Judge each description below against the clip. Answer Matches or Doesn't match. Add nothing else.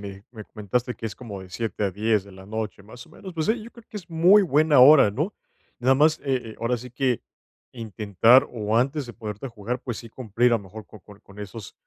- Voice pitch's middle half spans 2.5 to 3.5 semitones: Doesn't match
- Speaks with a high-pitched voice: Doesn't match